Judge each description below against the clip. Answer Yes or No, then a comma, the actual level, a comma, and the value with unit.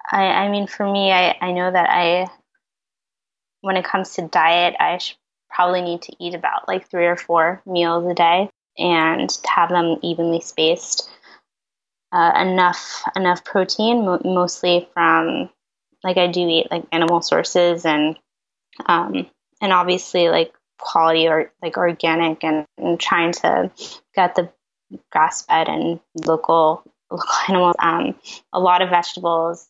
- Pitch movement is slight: Yes, narrow, 1.5 semitones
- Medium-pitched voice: Yes, medium, 175 Hz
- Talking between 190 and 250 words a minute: No, average, 145 wpm